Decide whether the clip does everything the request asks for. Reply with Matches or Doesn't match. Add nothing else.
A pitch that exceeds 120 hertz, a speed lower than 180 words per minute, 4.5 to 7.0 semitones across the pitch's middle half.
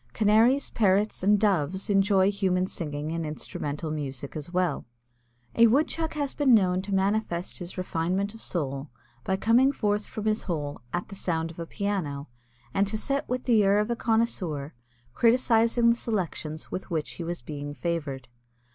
Matches